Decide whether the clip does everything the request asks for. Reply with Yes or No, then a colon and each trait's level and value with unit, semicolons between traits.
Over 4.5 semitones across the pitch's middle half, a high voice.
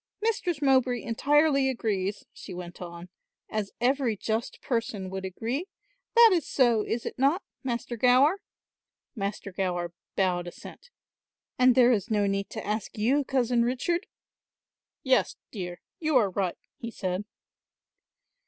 Yes: average, 5.3 semitones; high, 235 Hz